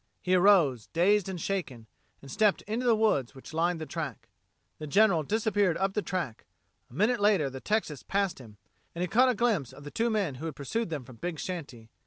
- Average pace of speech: No, fast, 215 wpm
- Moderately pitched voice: Yes, medium, 175 Hz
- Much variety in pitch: Yes, wide, 6.8 semitones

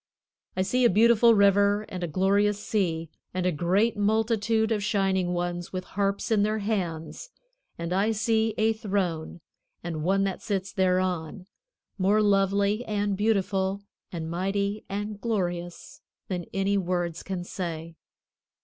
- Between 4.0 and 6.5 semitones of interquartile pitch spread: No, average, 2.7 semitones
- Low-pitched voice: No, high, 195 Hz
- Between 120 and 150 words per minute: Yes, average, 140 wpm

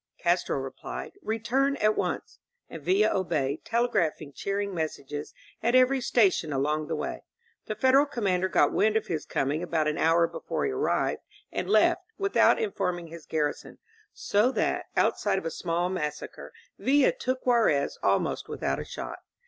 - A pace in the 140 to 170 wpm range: Yes, average, 160 wpm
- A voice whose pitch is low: No, medium, 185 Hz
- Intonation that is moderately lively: No, wide, 7.2 semitones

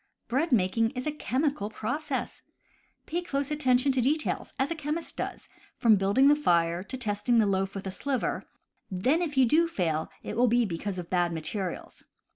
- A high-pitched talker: Yes, high, 245 Hz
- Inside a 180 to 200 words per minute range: Yes, average, 185 wpm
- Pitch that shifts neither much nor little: No, wide, 6.8 semitones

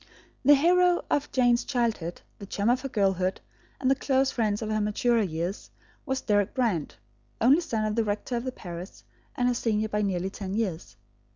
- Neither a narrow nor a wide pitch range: Yes, average, 4.3 semitones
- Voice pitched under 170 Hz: No, high, 220 Hz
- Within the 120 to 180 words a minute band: No, average, 190 wpm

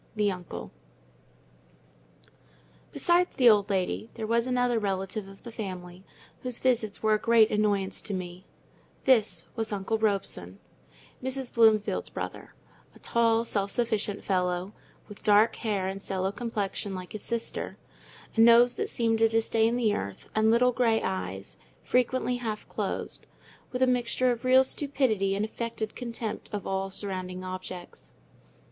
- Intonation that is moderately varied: Yes, average, 3.3 semitones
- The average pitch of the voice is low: No, high, 215 Hz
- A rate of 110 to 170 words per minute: Yes, average, 145 wpm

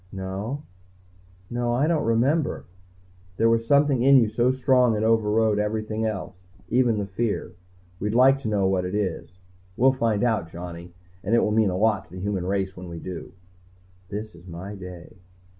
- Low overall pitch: Yes, low, 105 Hz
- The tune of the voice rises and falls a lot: No, average, 4.2 semitones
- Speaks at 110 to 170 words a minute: No, average, 185 wpm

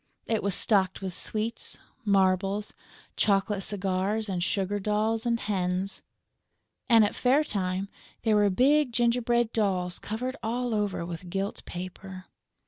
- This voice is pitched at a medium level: No, high, 205 Hz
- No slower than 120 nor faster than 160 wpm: Yes, slow, 135 wpm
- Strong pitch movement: No, average, 3.1 semitones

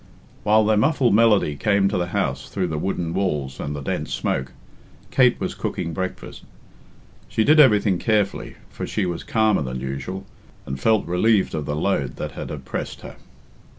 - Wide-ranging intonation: Yes, wide, 6.3 semitones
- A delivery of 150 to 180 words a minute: Yes, average, 175 wpm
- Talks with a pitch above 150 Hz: No, very low, 95 Hz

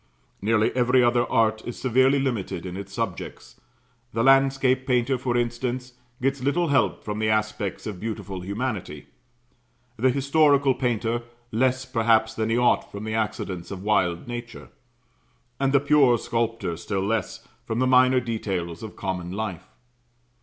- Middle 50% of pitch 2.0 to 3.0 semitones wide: No, average, 3.7 semitones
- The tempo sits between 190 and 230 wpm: No, average, 150 wpm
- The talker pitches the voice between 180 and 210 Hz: No, low, 115 Hz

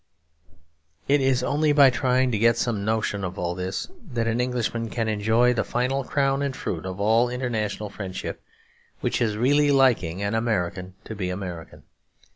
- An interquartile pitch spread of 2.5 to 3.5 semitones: No, average, 4.0 semitones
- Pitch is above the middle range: No, low, 115 Hz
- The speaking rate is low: No, average, 170 wpm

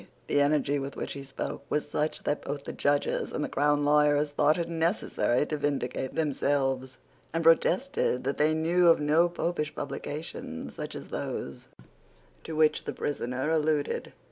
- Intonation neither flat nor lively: No, narrow, 1.9 semitones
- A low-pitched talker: No, medium, 150 Hz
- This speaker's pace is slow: No, average, 165 wpm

